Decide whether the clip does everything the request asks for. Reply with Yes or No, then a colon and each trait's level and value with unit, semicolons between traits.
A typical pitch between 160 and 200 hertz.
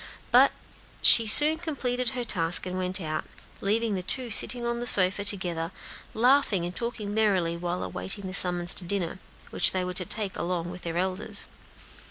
Yes: high, 190 Hz